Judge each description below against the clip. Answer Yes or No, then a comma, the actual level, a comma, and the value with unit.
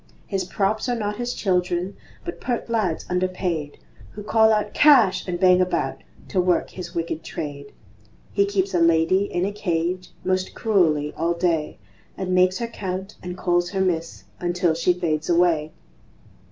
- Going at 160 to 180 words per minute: Yes, average, 165 wpm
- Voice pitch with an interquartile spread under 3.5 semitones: Yes, average, 2.7 semitones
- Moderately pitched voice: Yes, medium, 180 Hz